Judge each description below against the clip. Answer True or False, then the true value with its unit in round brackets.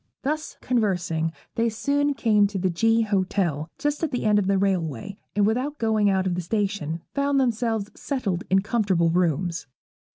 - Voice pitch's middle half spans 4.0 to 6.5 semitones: True (4.3 semitones)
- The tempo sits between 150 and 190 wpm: True (170 wpm)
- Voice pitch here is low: False (205 Hz)